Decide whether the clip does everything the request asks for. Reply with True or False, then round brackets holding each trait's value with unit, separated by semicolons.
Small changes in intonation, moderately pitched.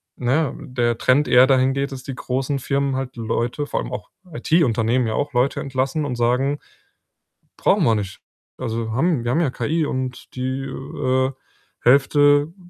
False (2.3 semitones; 130 Hz)